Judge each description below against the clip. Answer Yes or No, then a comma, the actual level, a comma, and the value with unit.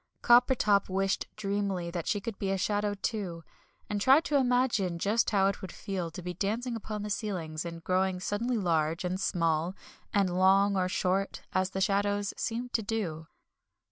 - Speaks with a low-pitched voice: No, high, 195 Hz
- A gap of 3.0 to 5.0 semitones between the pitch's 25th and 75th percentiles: No, narrow, 2.5 semitones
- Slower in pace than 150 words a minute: No, average, 175 wpm